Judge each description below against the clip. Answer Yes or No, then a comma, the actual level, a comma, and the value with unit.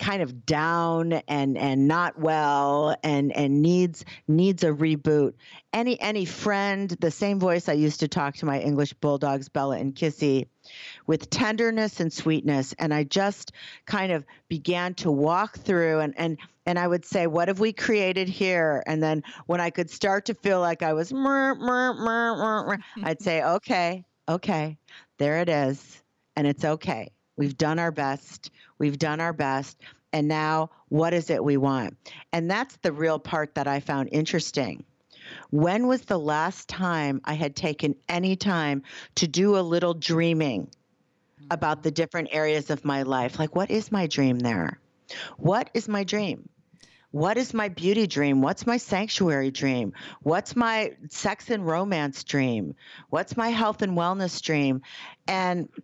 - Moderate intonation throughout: Yes, average, 4.3 semitones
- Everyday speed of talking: Yes, average, 170 wpm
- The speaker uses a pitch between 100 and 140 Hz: No, medium, 165 Hz